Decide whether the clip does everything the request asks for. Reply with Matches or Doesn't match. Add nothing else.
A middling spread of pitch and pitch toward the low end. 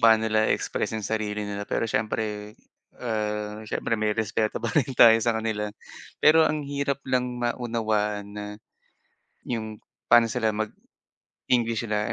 Doesn't match